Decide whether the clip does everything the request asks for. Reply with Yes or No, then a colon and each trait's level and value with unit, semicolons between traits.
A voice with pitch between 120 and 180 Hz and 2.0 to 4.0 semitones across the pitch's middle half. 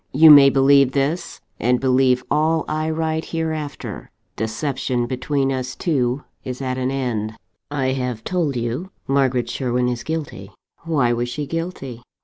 Yes: low, 135 Hz; average, 3.5 semitones